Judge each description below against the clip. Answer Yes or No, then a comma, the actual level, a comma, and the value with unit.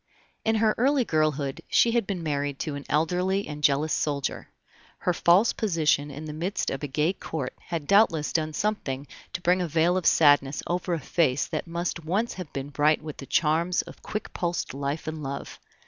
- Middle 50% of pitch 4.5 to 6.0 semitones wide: No, average, 3.7 semitones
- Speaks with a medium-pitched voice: Yes, medium, 160 Hz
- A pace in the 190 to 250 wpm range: Yes, average, 195 wpm